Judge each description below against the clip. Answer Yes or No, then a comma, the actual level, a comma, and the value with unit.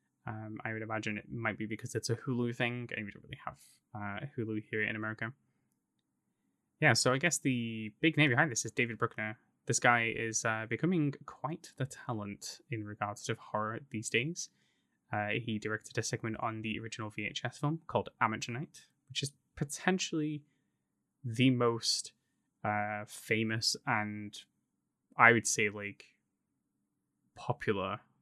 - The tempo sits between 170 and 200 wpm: No, average, 155 wpm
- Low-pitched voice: Yes, low, 115 Hz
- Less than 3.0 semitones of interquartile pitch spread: No, average, 3.5 semitones